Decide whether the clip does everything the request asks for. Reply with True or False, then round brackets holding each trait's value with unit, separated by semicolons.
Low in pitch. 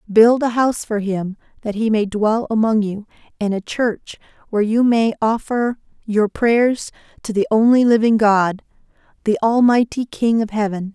False (220 Hz)